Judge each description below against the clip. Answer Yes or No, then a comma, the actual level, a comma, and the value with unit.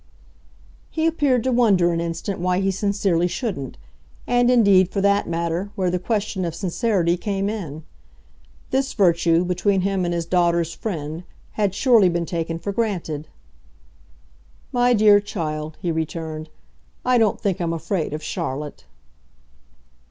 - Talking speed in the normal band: Yes, average, 145 wpm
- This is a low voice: No, medium, 180 Hz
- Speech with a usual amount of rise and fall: Yes, average, 3.7 semitones